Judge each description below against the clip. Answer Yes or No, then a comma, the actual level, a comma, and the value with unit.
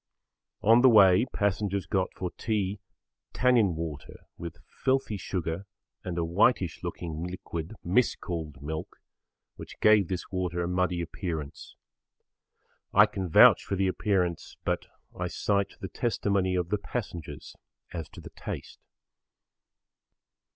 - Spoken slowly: Yes, slow, 130 wpm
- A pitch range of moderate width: Yes, average, 3.2 semitones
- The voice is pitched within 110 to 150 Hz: No, very low, 95 Hz